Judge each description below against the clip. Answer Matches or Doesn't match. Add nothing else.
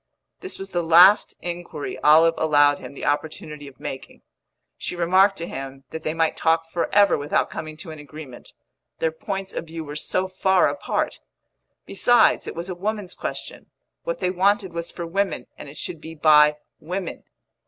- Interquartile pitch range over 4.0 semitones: Doesn't match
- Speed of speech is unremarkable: Matches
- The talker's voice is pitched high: Doesn't match